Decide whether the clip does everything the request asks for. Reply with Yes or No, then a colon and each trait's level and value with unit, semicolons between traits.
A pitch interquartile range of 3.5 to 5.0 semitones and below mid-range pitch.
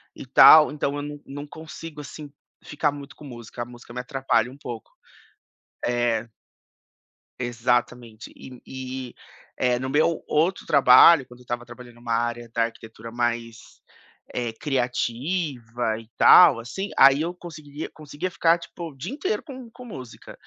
Yes: average, 4.0 semitones; low, 130 Hz